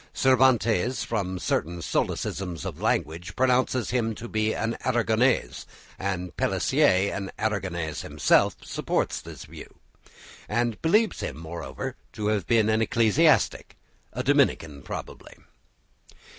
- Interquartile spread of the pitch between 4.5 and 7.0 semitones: Yes, average, 5.0 semitones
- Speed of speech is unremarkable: No, slow, 115 wpm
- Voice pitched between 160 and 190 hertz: No, low, 110 Hz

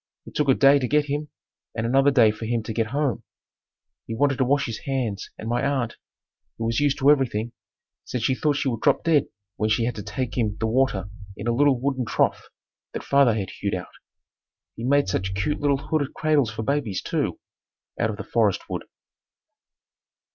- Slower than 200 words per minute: No, fast, 205 wpm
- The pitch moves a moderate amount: Yes, average, 4.1 semitones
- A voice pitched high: No, low, 125 Hz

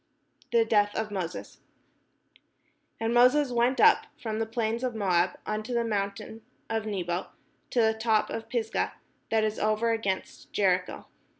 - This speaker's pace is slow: No, average, 145 wpm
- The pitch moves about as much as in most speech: No, narrow, 2.1 semitones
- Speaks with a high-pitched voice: Yes, high, 220 Hz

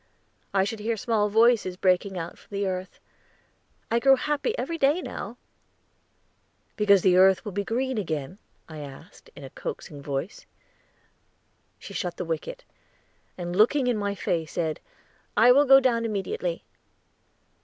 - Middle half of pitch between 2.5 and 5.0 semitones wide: No, wide, 5.4 semitones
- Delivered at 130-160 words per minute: Yes, average, 150 wpm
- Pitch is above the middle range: Yes, high, 205 Hz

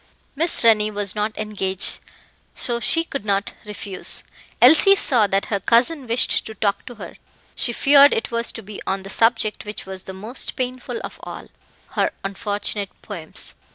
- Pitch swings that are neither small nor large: Yes, average, 3.4 semitones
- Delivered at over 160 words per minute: Yes, average, 170 wpm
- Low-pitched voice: No, high, 215 Hz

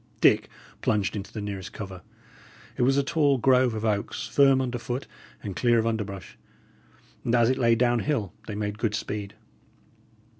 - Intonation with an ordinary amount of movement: Yes, average, 3.6 semitones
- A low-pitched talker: Yes, low, 115 Hz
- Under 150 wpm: No, average, 175 wpm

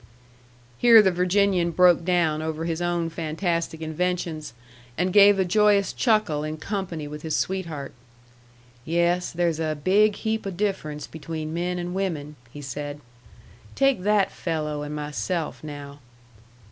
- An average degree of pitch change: Yes, average, 3.6 semitones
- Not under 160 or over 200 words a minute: No, average, 140 wpm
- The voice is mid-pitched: Yes, medium, 170 Hz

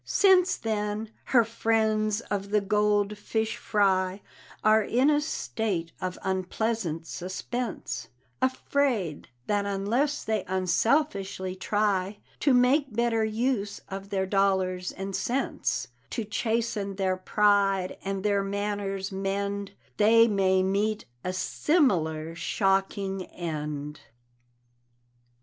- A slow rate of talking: Yes, slow, 110 wpm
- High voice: Yes, high, 200 Hz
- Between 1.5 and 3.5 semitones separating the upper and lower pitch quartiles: Yes, average, 2.7 semitones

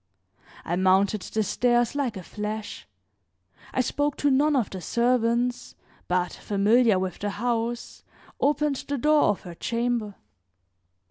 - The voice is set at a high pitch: Yes, high, 235 Hz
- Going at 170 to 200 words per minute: No, slow, 135 wpm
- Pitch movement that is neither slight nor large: Yes, average, 3.9 semitones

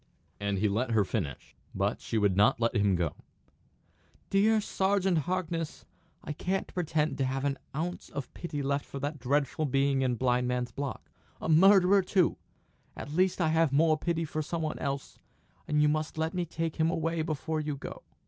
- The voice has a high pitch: No, medium, 150 Hz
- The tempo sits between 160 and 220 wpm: Yes, average, 185 wpm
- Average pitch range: Yes, average, 4.0 semitones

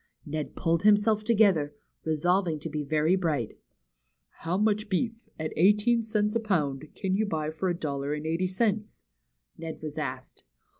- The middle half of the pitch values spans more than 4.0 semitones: Yes, average, 5.2 semitones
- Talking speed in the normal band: Yes, average, 165 wpm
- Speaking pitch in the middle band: Yes, medium, 175 Hz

